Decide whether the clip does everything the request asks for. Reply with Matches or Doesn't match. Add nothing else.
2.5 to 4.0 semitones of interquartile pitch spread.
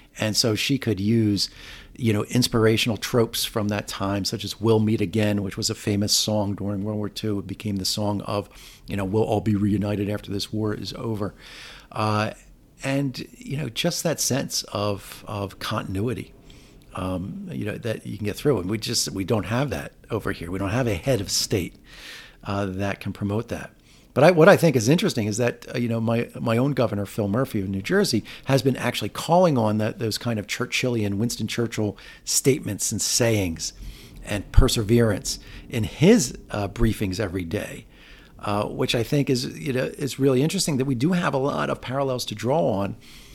Matches